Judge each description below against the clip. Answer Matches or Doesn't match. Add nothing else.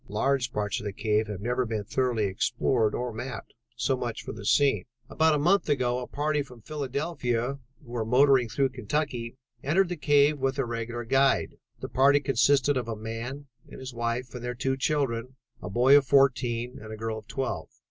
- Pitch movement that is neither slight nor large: Matches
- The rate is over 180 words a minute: Matches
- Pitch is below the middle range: Matches